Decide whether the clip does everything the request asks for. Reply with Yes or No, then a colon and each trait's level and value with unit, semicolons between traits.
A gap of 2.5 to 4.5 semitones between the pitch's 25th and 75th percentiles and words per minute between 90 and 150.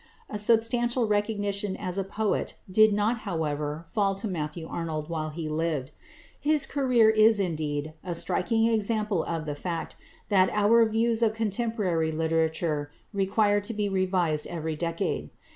No: average, 5.1 semitones; average, 145 wpm